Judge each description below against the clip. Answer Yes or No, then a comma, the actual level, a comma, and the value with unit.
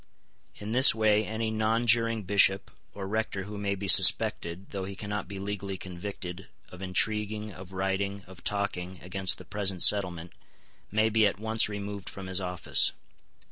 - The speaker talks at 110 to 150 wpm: No, average, 160 wpm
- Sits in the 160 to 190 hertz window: No, low, 100 Hz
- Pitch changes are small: Yes, narrow, 2.1 semitones